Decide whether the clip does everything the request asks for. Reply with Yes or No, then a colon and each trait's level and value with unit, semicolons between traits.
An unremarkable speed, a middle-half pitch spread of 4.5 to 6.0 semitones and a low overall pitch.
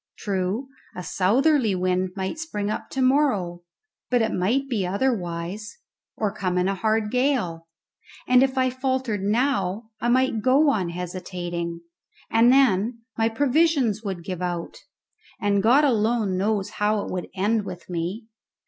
No: average, 150 wpm; wide, 5.5 semitones; high, 210 Hz